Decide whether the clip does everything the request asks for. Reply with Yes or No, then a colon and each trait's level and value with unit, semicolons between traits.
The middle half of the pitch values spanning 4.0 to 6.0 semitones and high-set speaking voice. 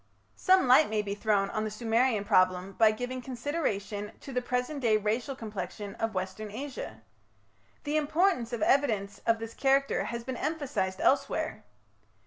Yes: average, 4.3 semitones; high, 225 Hz